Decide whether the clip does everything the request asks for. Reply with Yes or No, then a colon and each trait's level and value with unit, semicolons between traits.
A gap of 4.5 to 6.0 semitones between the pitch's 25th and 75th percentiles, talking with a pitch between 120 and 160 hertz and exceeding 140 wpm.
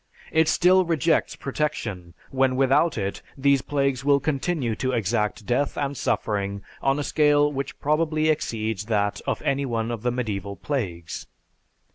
Yes: average, 5.2 semitones; low, 135 Hz; average, 150 wpm